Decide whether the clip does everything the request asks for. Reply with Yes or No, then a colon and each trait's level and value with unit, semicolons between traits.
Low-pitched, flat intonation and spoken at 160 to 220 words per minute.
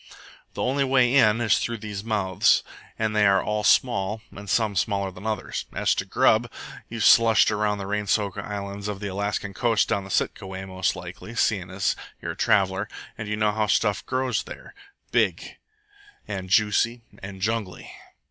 Yes: low, 105 Hz; narrow, 2.2 semitones; average, 180 wpm